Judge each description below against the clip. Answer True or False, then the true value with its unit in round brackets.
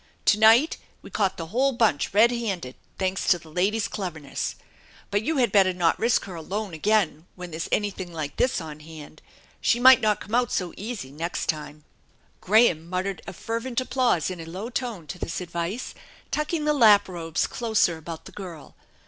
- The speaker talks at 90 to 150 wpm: False (190 wpm)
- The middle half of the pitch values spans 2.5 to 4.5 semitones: False (5.6 semitones)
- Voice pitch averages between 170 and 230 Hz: True (190 Hz)